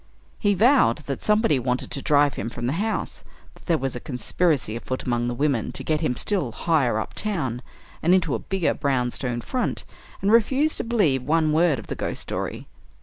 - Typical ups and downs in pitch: No, wide, 7.5 semitones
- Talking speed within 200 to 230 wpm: Yes, fast, 205 wpm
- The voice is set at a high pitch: No, medium, 150 Hz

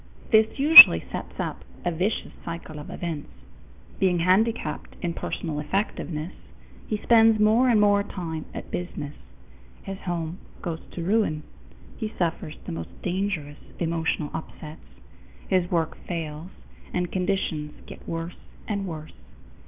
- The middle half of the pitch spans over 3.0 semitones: Yes, average, 4.0 semitones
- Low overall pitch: No, medium, 175 Hz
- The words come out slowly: Yes, slow, 130 wpm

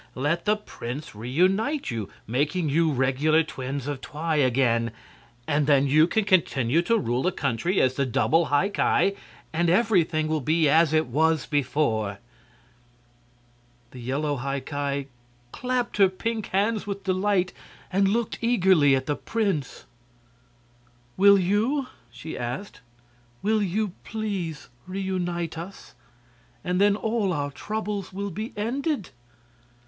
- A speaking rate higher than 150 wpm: No, slow, 135 wpm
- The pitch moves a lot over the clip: Yes, wide, 6.2 semitones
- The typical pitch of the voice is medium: Yes, medium, 165 Hz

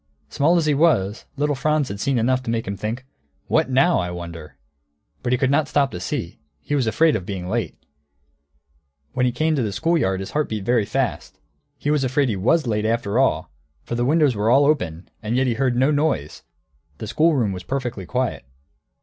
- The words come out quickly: Yes, fast, 210 wpm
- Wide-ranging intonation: Yes, wide, 6.0 semitones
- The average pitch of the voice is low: Yes, low, 125 Hz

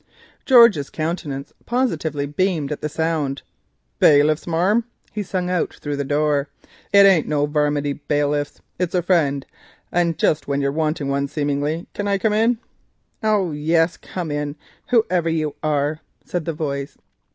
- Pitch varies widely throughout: No, average, 3.7 semitones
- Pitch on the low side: No, medium, 155 Hz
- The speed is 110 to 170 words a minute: Yes, average, 150 wpm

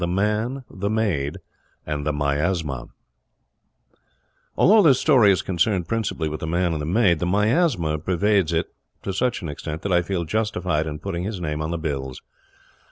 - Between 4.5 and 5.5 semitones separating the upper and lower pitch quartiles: Yes, average, 5.2 semitones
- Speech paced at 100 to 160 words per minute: No, average, 175 wpm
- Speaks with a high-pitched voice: No, very low, 90 Hz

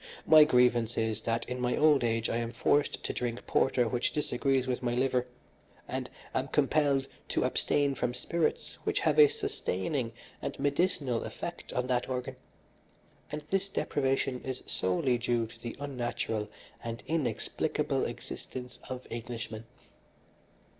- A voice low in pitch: Yes, low, 125 Hz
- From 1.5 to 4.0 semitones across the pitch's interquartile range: Yes, average, 3.2 semitones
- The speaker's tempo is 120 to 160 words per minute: Yes, average, 145 wpm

